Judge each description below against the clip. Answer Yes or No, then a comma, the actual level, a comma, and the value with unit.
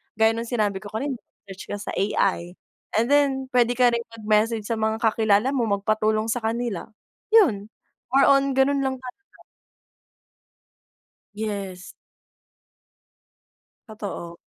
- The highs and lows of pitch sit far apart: No, average, 3.4 semitones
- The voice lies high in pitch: Yes, high, 225 Hz